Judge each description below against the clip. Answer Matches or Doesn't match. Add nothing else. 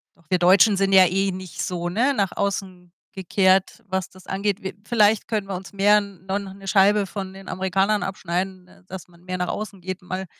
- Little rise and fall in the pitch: Matches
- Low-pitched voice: Doesn't match